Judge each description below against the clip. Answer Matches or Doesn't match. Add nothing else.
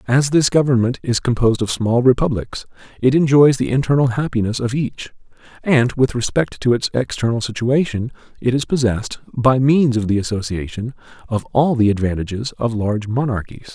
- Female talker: Doesn't match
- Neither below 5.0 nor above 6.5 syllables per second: Matches